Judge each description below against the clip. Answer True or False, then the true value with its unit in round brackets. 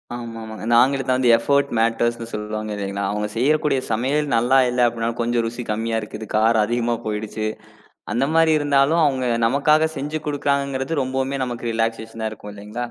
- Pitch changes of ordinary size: True (3.6 semitones)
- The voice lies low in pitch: True (120 Hz)